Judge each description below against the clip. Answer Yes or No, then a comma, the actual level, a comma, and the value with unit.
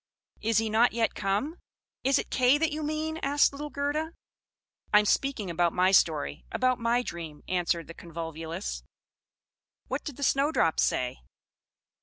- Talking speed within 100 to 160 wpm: Yes, average, 155 wpm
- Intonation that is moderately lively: No, wide, 8.8 semitones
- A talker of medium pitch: No, high, 225 Hz